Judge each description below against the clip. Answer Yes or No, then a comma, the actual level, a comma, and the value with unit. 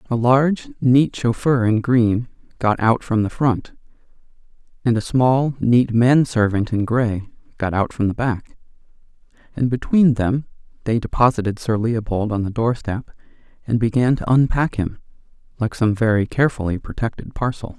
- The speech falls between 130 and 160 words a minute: Yes, average, 150 wpm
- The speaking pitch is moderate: No, low, 115 Hz